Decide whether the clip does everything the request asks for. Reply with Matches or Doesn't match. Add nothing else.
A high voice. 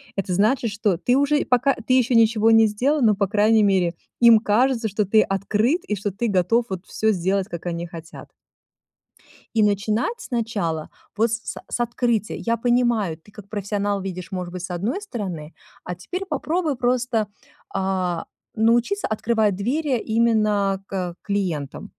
Matches